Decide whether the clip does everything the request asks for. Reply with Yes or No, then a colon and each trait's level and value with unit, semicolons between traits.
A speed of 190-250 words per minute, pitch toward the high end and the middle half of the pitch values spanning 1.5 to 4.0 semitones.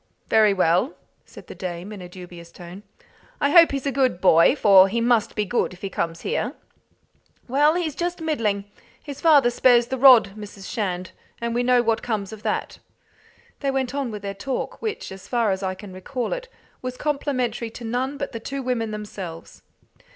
No: average, 195 wpm; high, 230 Hz; wide, 5.5 semitones